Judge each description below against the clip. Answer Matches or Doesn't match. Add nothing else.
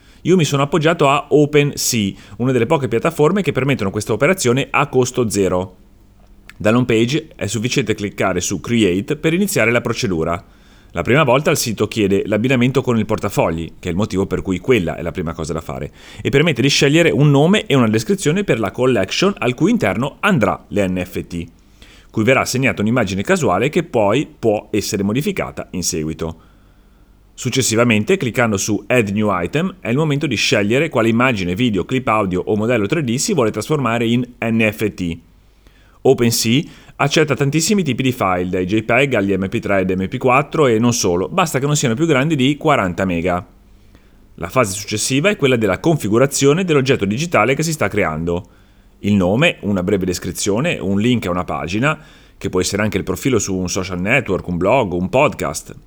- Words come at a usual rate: Doesn't match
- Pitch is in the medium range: Doesn't match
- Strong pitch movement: Matches